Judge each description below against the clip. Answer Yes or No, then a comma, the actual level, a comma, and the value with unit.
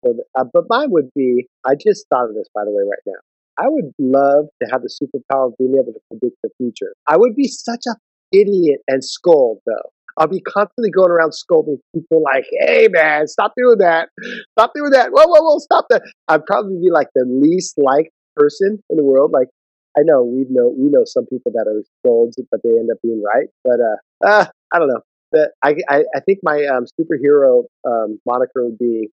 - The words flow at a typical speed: No, fast, 220 wpm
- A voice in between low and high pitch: Yes, medium, 165 Hz